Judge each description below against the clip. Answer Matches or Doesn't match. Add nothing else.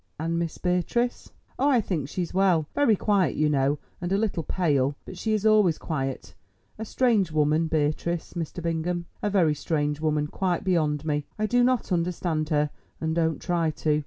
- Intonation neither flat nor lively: Matches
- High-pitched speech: Doesn't match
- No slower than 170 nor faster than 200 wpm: Matches